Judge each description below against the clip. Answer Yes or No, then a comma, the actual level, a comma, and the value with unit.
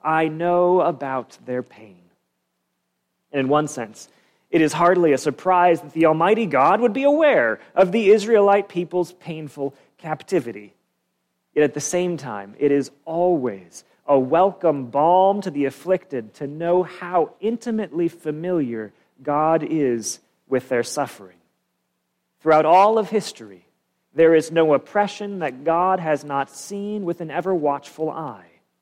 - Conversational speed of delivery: Yes, average, 145 wpm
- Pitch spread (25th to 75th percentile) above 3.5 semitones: Yes, average, 4.8 semitones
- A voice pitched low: No, medium, 160 Hz